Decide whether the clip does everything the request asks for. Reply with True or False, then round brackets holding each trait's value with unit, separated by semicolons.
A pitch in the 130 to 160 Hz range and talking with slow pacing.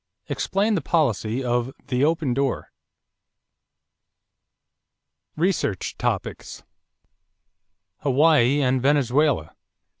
True (140 Hz; 70 wpm)